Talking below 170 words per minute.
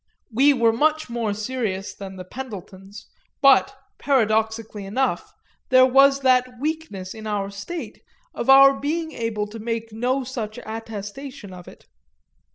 Yes: average, 140 wpm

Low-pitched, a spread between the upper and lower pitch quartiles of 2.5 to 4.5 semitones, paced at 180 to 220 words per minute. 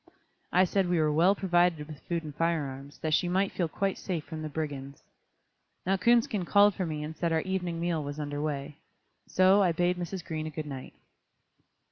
No: medium, 165 Hz; average, 3.3 semitones; fast, 205 wpm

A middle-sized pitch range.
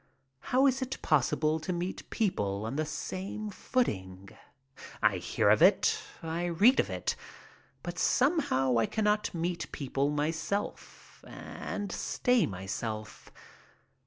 No: wide, 8.3 semitones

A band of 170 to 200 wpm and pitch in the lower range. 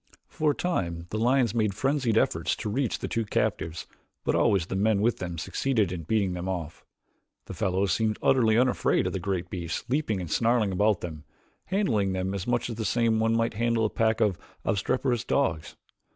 Yes: average, 195 wpm; low, 110 Hz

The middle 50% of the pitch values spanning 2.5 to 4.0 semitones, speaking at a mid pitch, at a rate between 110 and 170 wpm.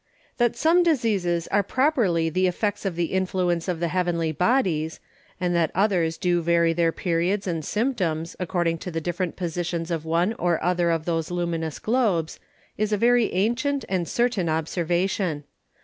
Yes: average, 3.5 semitones; medium, 175 Hz; average, 165 wpm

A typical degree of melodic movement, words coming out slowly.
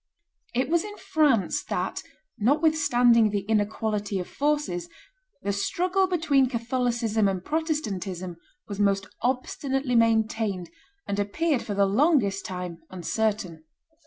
No: wide, 6.2 semitones; slow, 115 wpm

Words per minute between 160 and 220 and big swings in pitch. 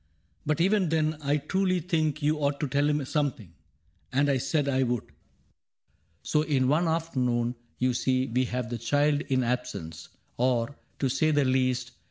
No: average, 185 wpm; average, 3.4 semitones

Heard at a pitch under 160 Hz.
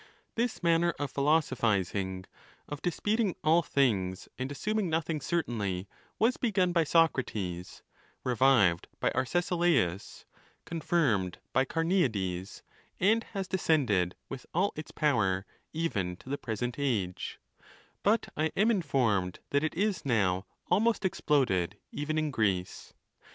Yes: medium, 140 Hz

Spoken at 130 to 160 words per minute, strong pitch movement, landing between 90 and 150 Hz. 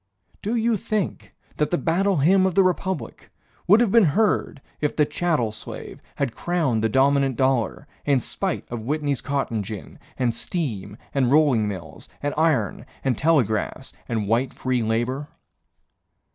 Yes: average, 155 wpm; wide, 6.7 semitones; medium, 140 Hz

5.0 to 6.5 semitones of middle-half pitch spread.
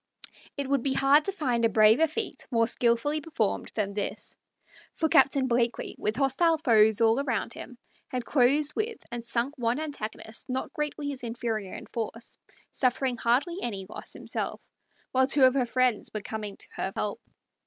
No: average, 3.8 semitones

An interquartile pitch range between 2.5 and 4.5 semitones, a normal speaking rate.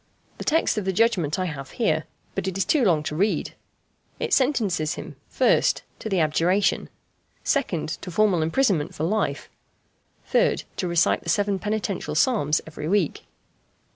No: average, 5.2 semitones; average, 160 wpm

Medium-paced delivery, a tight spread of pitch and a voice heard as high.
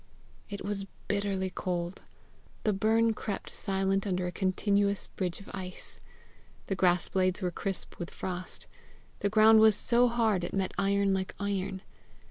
Yes: average, 150 wpm; narrow, 1.6 semitones; high, 195 Hz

